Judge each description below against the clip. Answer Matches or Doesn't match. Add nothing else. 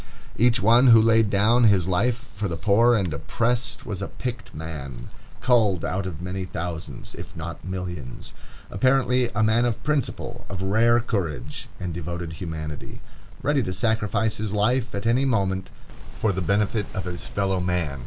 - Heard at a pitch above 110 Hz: Doesn't match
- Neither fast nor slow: Matches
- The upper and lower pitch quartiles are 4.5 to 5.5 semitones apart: Matches